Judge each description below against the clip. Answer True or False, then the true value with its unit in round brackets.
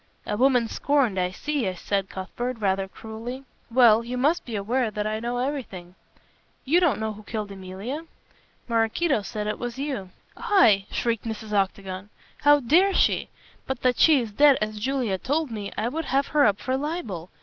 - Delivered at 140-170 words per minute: False (180 wpm)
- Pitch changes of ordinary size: True (4.8 semitones)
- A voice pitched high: True (230 Hz)